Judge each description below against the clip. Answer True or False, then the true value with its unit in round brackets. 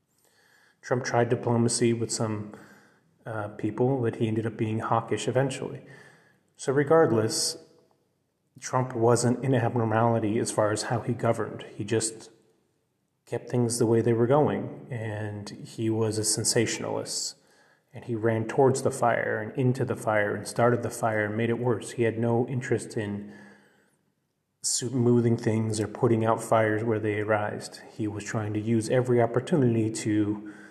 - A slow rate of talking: False (155 wpm)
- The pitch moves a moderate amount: False (2.0 semitones)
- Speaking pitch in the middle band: False (115 Hz)